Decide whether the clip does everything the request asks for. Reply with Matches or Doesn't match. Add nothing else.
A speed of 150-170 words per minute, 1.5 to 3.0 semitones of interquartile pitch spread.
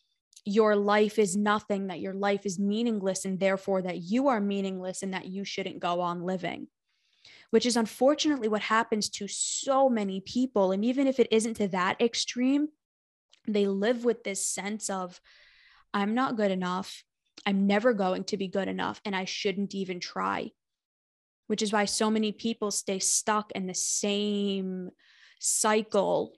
Matches